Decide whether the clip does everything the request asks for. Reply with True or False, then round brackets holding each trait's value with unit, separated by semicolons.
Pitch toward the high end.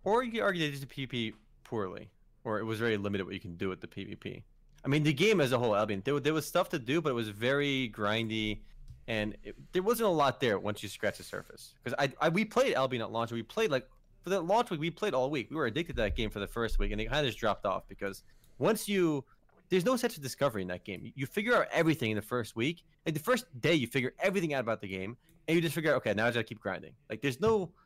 False (130 Hz)